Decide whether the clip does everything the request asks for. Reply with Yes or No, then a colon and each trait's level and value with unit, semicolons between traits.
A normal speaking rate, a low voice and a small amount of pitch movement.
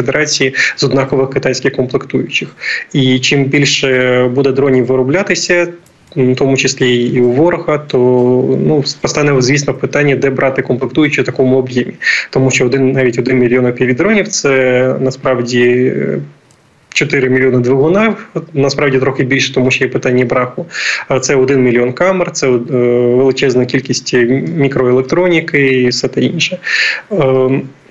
Yes: average, 135 wpm; low, 130 Hz; narrow, 1.9 semitones